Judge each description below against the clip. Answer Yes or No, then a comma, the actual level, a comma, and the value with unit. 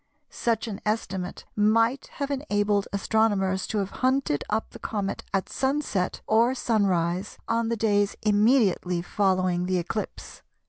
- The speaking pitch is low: No, high, 205 Hz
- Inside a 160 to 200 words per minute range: No, slow, 135 wpm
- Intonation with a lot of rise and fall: No, average, 3.2 semitones